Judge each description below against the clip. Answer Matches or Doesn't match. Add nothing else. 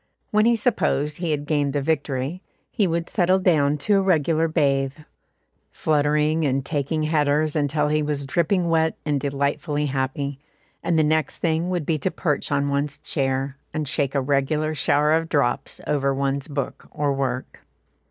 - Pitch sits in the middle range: Matches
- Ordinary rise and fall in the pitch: Doesn't match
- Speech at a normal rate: Matches